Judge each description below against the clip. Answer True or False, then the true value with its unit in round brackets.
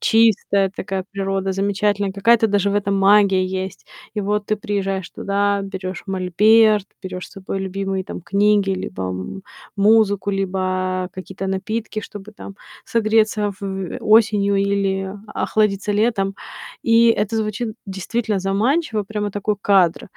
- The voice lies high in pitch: True (200 Hz)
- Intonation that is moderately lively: False (1.7 semitones)